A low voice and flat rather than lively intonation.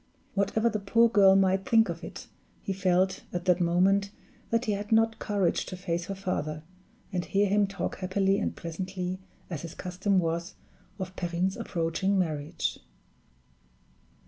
No: high, 190 Hz; narrow, 2.2 semitones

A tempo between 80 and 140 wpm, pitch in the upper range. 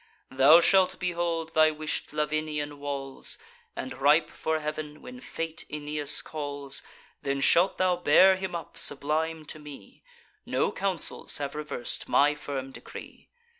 No: slow, 135 wpm; medium, 150 Hz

